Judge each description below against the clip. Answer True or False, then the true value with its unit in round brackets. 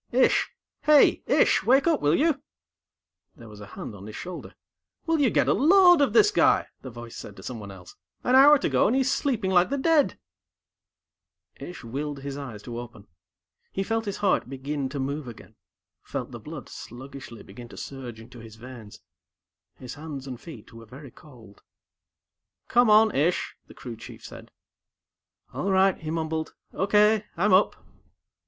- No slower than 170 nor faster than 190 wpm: True (175 wpm)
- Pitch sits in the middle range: True (145 Hz)